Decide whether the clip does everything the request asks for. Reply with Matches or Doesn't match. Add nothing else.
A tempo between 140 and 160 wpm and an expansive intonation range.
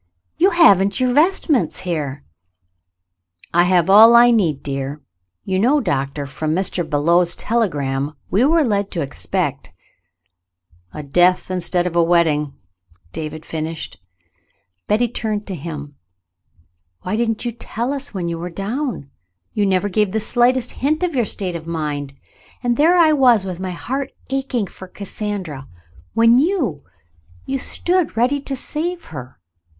Matches